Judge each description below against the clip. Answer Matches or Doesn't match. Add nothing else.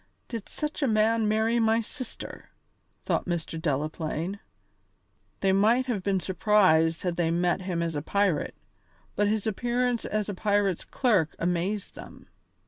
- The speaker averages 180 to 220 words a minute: Doesn't match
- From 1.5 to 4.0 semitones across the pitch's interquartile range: Doesn't match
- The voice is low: Doesn't match